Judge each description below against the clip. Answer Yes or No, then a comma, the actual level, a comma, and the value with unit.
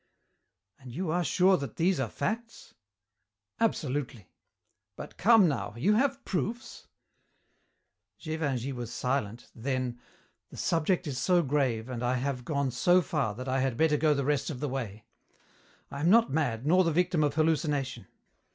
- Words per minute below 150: No, average, 160 wpm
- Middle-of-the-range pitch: Yes, medium, 145 Hz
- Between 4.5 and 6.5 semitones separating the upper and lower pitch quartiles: Yes, wide, 5.5 semitones